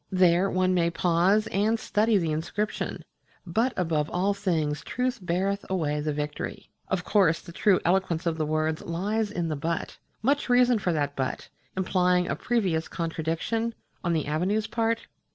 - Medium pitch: Yes, medium, 180 Hz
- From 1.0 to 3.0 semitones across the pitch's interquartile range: No, average, 4.2 semitones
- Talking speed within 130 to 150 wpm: No, average, 165 wpm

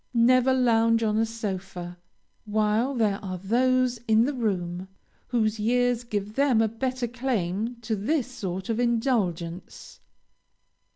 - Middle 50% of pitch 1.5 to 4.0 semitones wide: Yes, average, 3.7 semitones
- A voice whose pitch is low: No, high, 225 Hz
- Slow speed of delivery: Yes, slow, 130 wpm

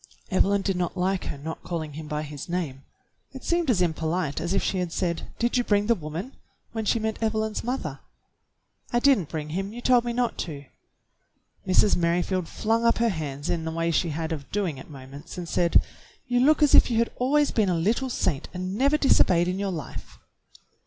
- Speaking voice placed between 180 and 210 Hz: Yes, medium, 185 Hz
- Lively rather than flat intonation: Yes, wide, 6.1 semitones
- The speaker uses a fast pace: Yes, fast, 215 wpm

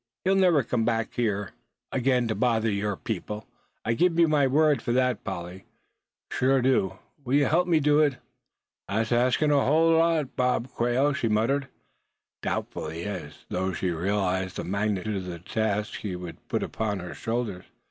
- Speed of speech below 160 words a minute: No, average, 175 wpm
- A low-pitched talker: Yes, low, 115 Hz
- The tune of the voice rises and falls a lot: Yes, wide, 5.7 semitones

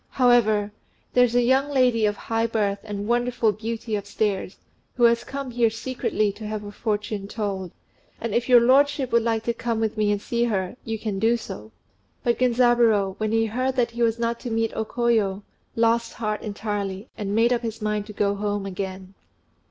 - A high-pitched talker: Yes, high, 225 Hz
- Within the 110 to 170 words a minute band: No, average, 195 wpm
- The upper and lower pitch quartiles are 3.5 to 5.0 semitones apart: No, narrow, 2.4 semitones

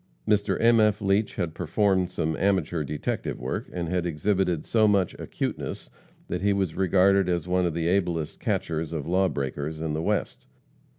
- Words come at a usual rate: Yes, average, 170 wpm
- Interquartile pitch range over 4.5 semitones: No, average, 3.4 semitones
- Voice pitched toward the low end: Yes, very low, 90 Hz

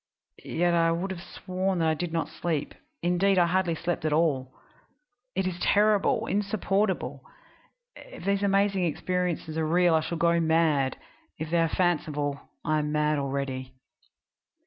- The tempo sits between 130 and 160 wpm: Yes, average, 155 wpm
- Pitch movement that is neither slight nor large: Yes, average, 3.1 semitones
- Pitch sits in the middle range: Yes, medium, 170 Hz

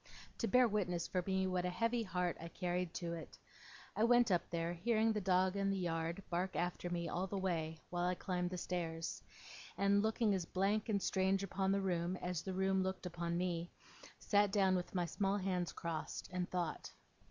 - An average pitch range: No, narrow, 2.1 semitones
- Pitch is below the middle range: No, medium, 185 Hz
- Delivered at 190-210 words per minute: Yes, average, 200 wpm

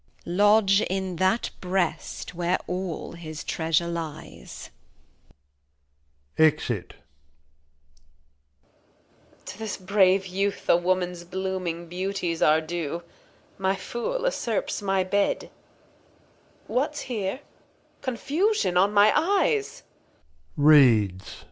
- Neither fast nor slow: No, slow, 90 wpm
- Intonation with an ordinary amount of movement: Yes, average, 4.2 semitones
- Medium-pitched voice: Yes, medium, 180 Hz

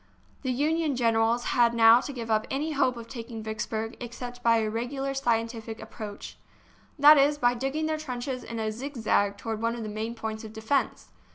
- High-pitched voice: Yes, high, 235 Hz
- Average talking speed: Yes, average, 190 wpm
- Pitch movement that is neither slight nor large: Yes, average, 3.3 semitones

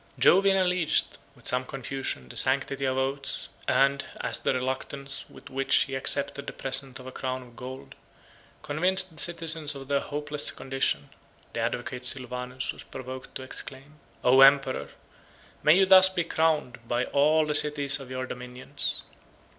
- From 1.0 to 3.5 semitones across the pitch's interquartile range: Yes, narrow, 2.5 semitones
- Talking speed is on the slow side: No, average, 160 wpm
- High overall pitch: No, low, 135 Hz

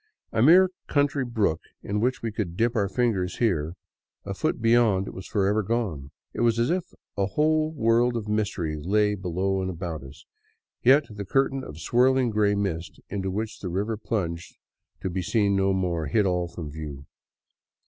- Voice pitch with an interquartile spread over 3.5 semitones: Yes, average, 4.5 semitones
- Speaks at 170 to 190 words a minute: Yes, average, 180 wpm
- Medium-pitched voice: No, low, 105 Hz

